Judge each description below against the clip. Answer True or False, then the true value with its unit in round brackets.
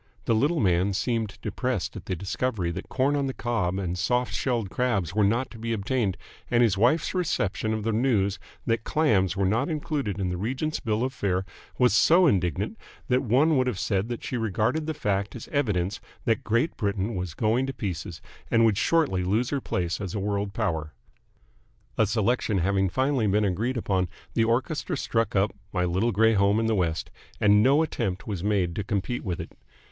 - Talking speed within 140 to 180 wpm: False (200 wpm)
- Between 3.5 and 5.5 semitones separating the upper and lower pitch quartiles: True (4.4 semitones)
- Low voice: True (110 Hz)